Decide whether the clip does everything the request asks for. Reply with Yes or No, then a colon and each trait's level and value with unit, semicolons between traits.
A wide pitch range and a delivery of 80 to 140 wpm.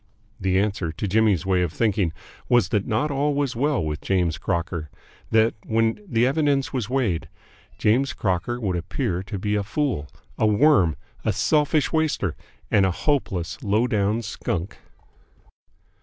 No: wide, 5.8 semitones; average, 155 wpm